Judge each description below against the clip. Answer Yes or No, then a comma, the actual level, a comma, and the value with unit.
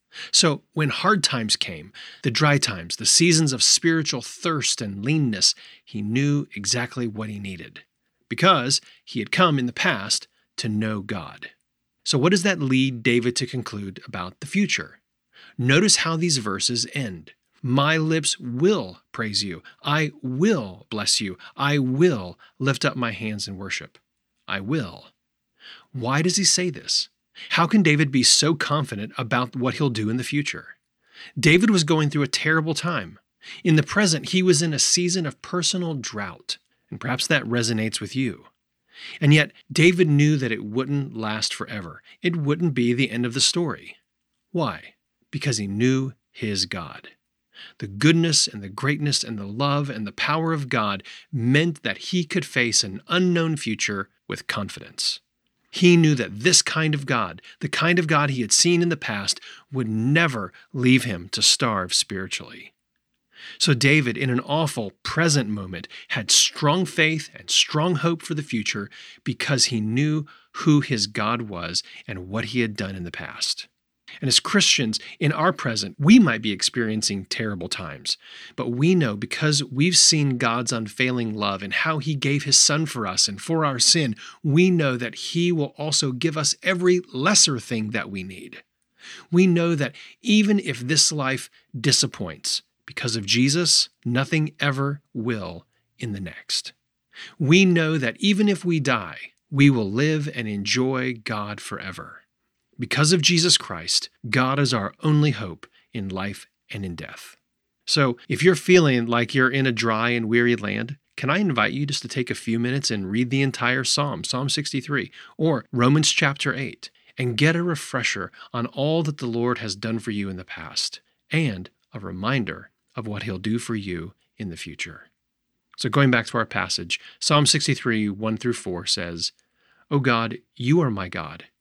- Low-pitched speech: Yes, low, 130 Hz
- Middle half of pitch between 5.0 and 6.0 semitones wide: Yes, wide, 5.6 semitones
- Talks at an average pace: Yes, average, 175 wpm